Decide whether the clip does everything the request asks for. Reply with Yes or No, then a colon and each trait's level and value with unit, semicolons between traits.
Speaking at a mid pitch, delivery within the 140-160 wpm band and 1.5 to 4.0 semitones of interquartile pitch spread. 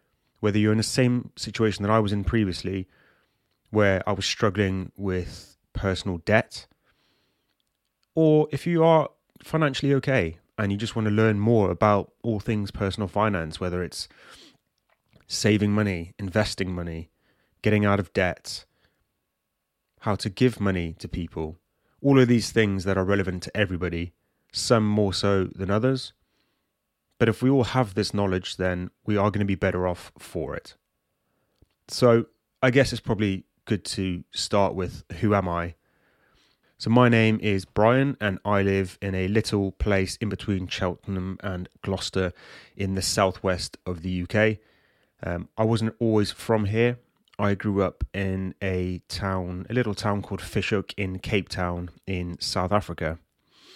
No: low, 100 Hz; average, 155 wpm; average, 3.1 semitones